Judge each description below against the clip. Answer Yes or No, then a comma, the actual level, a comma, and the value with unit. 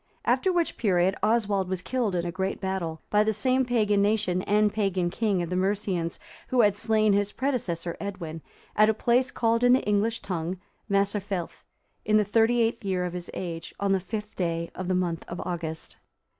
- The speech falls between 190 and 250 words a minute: Yes, average, 195 wpm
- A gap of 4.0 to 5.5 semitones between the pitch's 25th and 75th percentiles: No, average, 3.3 semitones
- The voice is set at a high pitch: Yes, high, 200 Hz